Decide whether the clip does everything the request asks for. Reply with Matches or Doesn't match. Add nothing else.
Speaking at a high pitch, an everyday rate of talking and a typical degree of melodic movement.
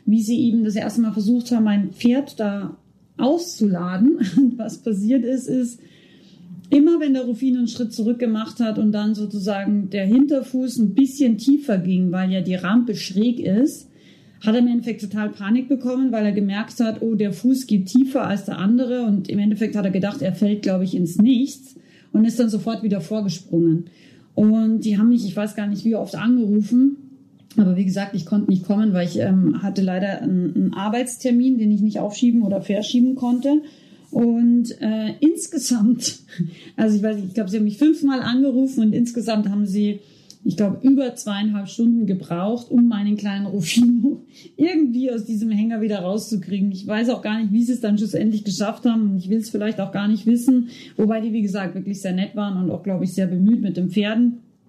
Doesn't match